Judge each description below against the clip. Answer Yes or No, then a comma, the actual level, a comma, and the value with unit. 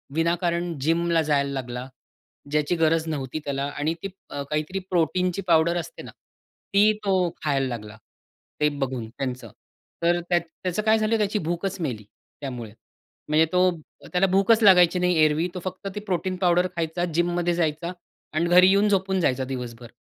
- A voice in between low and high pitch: Yes, medium, 170 Hz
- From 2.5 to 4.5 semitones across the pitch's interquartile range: Yes, average, 3.8 semitones